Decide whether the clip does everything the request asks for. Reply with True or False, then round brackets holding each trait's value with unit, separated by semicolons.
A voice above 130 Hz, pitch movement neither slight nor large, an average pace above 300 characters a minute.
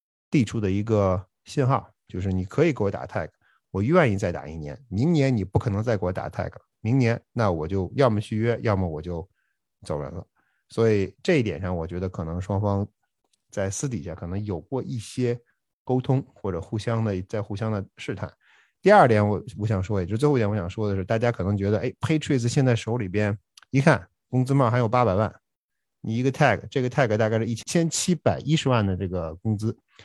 False (110 Hz; 4.4 semitones; 330 characters per minute)